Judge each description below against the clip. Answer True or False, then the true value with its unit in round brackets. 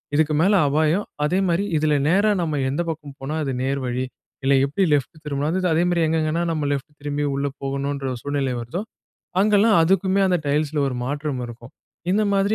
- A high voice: False (150 Hz)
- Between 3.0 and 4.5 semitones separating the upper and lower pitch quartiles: True (4.0 semitones)